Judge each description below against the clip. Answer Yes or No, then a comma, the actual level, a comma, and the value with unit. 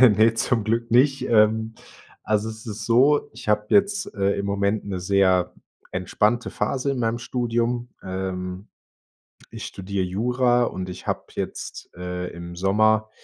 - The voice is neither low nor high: No, low, 110 Hz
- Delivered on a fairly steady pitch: No, average, 3.8 semitones